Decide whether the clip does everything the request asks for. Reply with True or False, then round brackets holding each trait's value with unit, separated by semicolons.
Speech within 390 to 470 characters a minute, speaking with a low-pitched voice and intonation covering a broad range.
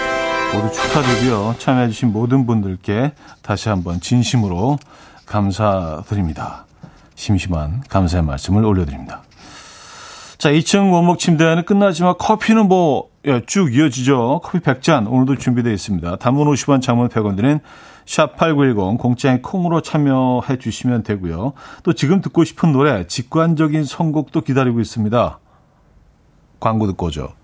False (295 characters per minute; 125 Hz; 6.7 semitones)